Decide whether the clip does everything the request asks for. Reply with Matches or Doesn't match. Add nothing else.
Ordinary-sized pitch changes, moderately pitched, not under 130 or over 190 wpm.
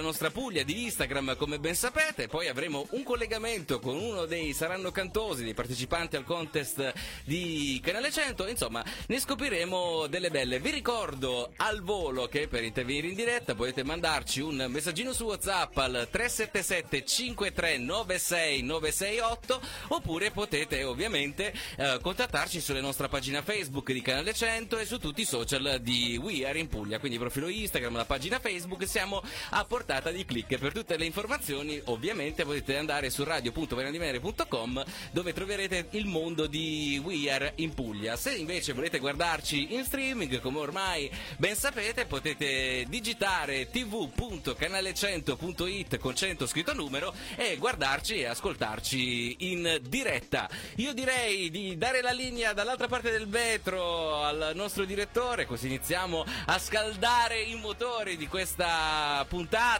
Doesn't match